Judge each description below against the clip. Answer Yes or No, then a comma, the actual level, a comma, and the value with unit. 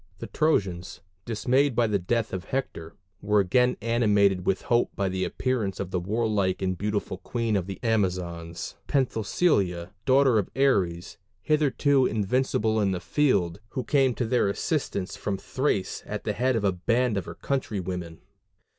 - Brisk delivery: No, average, 165 wpm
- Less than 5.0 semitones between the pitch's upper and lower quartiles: No, average, 5.3 semitones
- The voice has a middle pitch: No, low, 105 Hz